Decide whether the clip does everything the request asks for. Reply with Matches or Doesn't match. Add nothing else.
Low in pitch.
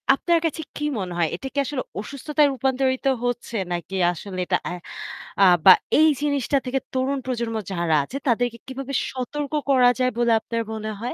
Doesn't match